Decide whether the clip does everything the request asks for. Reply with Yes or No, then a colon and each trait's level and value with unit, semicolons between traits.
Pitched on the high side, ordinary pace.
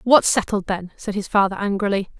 Yes: high, 200 Hz; average, 190 wpm